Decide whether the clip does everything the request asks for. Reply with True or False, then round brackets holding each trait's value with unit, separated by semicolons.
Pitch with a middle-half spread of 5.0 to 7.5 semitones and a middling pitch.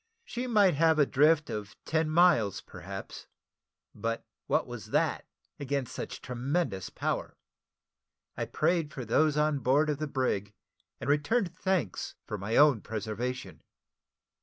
True (5.5 semitones; 145 Hz)